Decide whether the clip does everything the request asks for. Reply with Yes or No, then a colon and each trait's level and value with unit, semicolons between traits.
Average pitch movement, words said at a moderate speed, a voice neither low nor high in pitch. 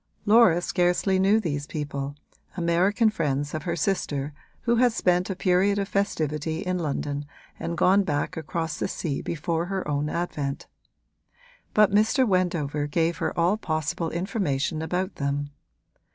Yes: average, 4.5 semitones; average, 145 wpm; medium, 170 Hz